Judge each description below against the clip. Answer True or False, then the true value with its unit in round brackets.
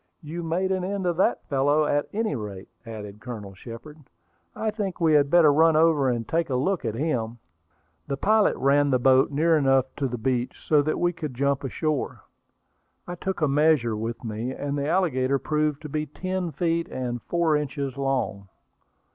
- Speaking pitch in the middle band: True (145 Hz)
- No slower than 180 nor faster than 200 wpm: True (190 wpm)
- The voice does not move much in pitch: False (4.2 semitones)